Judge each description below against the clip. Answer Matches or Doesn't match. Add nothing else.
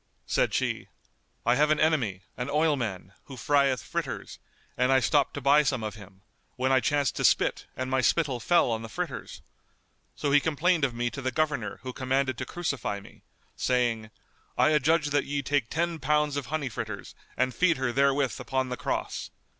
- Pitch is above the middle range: Doesn't match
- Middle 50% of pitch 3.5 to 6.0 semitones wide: Doesn't match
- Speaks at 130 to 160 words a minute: Doesn't match